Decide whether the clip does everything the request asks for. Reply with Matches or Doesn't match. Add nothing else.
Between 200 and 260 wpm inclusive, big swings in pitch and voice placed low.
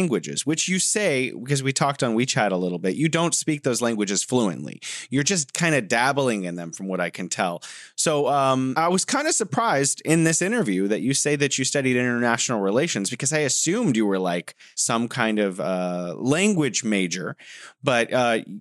Matches